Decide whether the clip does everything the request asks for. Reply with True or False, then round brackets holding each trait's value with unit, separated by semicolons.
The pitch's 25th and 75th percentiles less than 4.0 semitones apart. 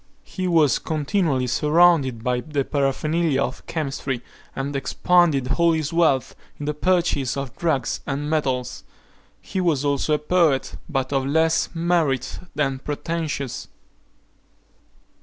True (3.5 semitones)